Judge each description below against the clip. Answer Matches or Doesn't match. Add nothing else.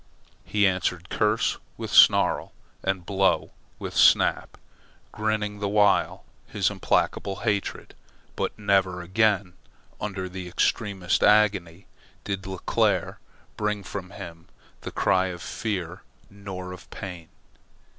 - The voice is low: Matches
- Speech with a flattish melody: Matches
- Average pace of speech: Doesn't match